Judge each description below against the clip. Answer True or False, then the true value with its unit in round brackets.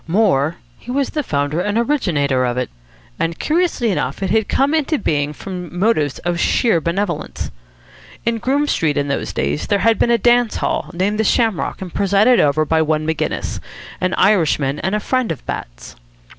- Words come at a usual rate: True (185 wpm)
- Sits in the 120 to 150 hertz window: False (185 Hz)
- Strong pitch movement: True (7.2 semitones)